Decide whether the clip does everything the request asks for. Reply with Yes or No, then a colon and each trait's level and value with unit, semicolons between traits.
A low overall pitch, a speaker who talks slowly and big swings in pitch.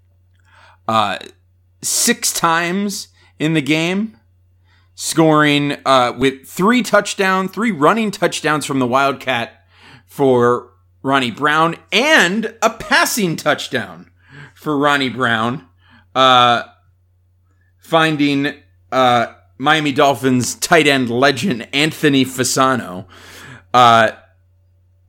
Yes: low, 130 Hz; slow, 90 wpm; wide, 8.7 semitones